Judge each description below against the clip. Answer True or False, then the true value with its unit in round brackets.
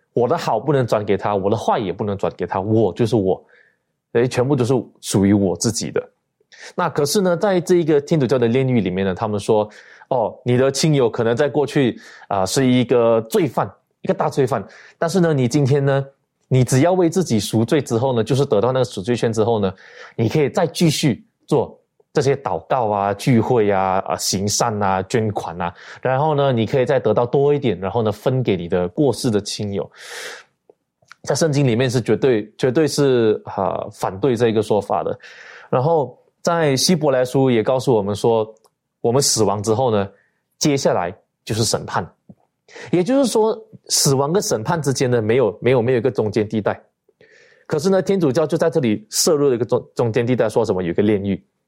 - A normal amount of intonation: False (6.0 semitones)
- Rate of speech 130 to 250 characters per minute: False (290 characters per minute)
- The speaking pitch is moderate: False (130 Hz)